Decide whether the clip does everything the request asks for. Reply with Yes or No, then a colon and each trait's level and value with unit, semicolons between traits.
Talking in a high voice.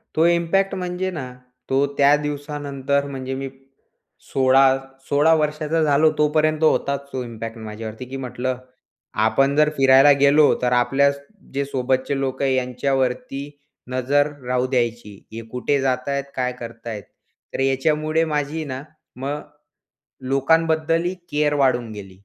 No: low, 135 Hz